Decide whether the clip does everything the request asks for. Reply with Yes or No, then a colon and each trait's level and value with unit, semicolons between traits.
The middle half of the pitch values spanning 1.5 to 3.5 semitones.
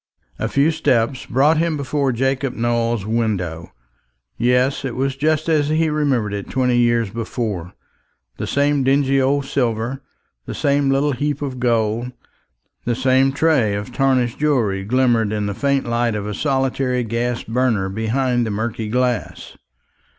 Yes: average, 3.2 semitones